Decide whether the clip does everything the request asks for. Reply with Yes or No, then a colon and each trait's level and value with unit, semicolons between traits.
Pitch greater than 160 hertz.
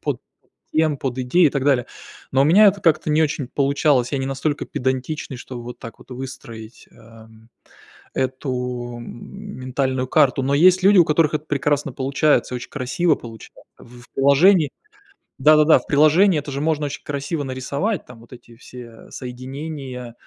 No: low, 135 Hz